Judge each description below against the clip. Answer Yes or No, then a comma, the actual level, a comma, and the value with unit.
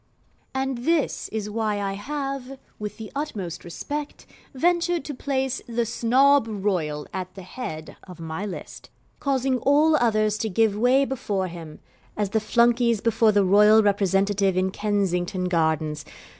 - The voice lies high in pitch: Yes, high, 215 Hz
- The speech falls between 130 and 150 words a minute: Yes, average, 145 wpm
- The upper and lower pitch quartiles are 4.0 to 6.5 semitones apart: Yes, wide, 5.6 semitones